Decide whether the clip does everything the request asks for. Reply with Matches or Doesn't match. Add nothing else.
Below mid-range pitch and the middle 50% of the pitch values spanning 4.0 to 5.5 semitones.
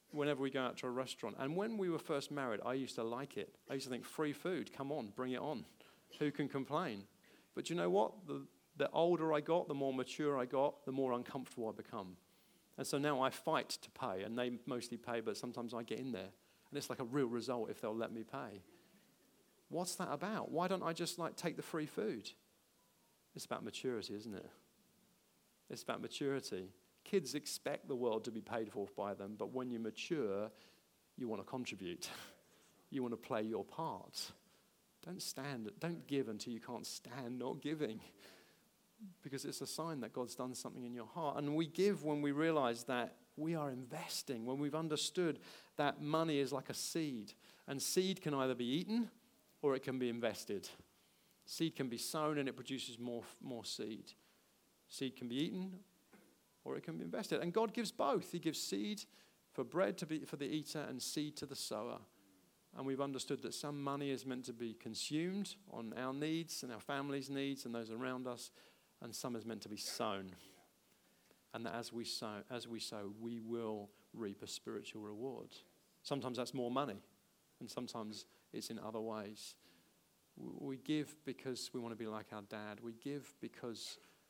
Matches